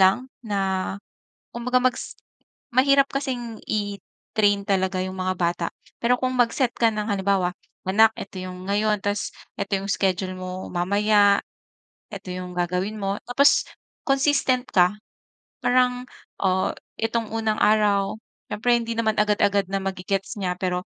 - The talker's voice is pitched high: Yes, high, 205 Hz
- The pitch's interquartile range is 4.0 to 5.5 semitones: No, average, 3.5 semitones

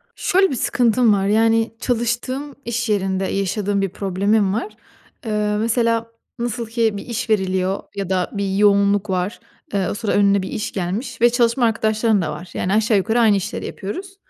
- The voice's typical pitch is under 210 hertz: No, high, 215 Hz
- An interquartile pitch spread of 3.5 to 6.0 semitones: No, average, 3.0 semitones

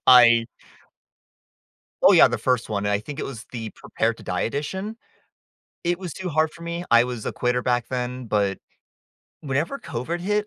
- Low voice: Yes, low, 125 Hz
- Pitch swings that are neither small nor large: No, wide, 6.5 semitones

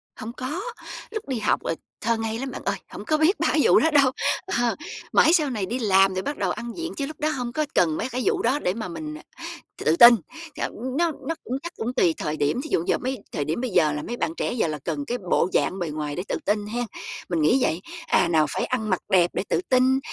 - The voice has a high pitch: Yes, high, 235 Hz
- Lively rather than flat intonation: Yes, wide, 7.6 semitones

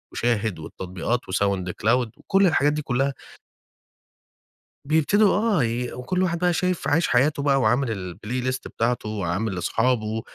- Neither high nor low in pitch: No, low, 125 Hz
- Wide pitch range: Yes, wide, 5.8 semitones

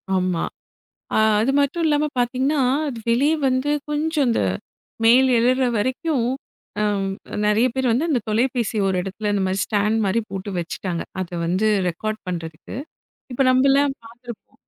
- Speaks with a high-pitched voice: Yes, high, 235 Hz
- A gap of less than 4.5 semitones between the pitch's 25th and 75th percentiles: No, average, 4.8 semitones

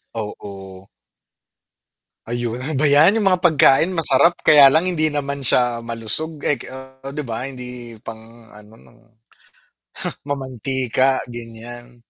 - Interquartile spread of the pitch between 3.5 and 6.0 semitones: Yes, average, 4.1 semitones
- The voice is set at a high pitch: No, low, 125 Hz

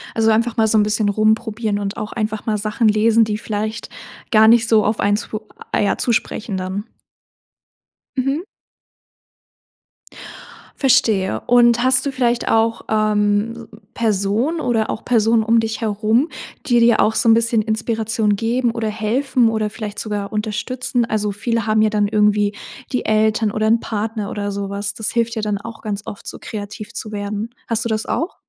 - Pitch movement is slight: Yes, narrow, 1.7 semitones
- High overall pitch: Yes, high, 220 Hz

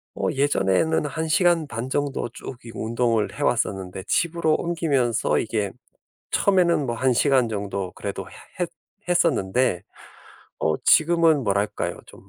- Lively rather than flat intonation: Yes, wide, 7.1 semitones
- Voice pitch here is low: Yes, low, 130 Hz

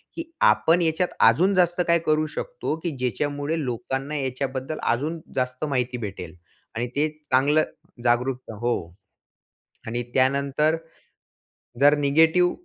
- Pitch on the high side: No, medium, 140 Hz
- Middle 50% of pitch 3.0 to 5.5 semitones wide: Yes, average, 4.0 semitones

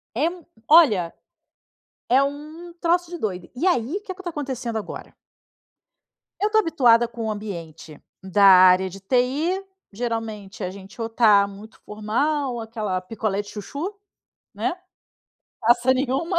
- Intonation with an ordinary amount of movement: No, wide, 7.1 semitones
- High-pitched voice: Yes, high, 235 Hz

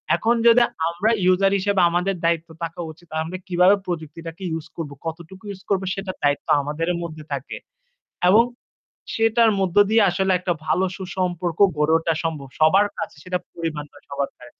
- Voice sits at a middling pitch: Yes, medium, 175 Hz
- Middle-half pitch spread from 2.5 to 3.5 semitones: Yes, average, 3.1 semitones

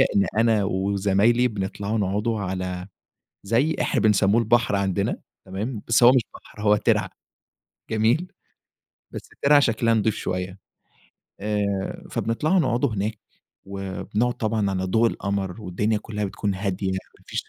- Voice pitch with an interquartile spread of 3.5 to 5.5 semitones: No, average, 2.8 semitones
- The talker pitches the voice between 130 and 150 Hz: No, low, 105 Hz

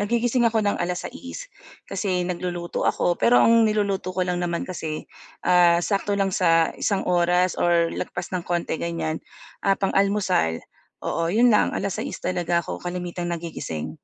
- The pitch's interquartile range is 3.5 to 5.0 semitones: No, average, 2.7 semitones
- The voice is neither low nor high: Yes, medium, 180 Hz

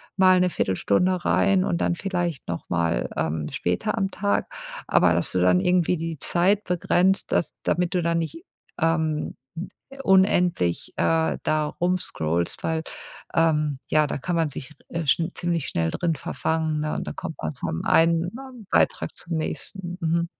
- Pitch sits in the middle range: Yes, medium, 165 Hz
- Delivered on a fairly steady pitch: No, average, 3.0 semitones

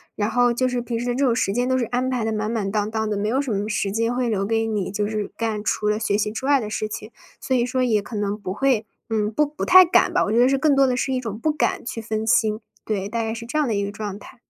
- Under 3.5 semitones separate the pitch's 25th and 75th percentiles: Yes, average, 3.0 semitones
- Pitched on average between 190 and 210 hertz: No, high, 225 Hz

